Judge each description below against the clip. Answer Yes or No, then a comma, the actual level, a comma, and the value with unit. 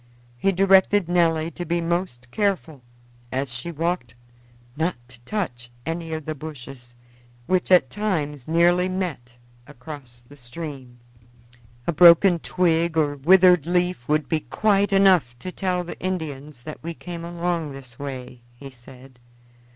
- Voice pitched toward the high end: No, medium, 160 Hz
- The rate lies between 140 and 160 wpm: Yes, average, 145 wpm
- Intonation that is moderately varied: Yes, average, 5.0 semitones